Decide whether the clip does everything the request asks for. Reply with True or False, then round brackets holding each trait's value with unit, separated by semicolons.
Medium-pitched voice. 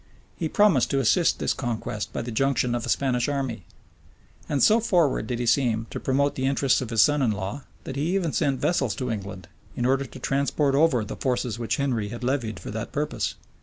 False (130 Hz)